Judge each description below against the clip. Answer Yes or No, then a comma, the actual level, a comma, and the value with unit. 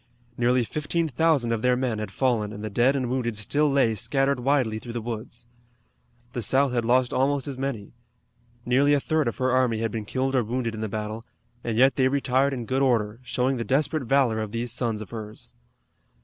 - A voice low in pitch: Yes, low, 125 Hz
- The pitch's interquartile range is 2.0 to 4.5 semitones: Yes, average, 3.0 semitones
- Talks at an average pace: No, fast, 210 wpm